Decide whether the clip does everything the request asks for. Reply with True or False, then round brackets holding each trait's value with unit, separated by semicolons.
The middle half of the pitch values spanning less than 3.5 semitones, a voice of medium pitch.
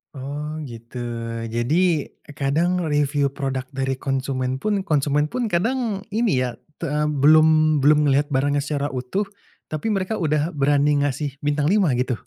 True (2.8 semitones; 145 Hz)